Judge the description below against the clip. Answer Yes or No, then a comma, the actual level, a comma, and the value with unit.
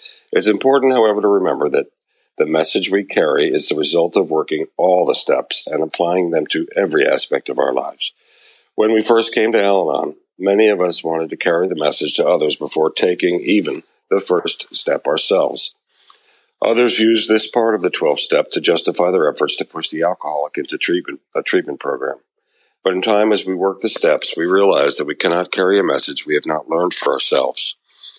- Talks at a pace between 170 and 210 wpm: Yes, average, 195 wpm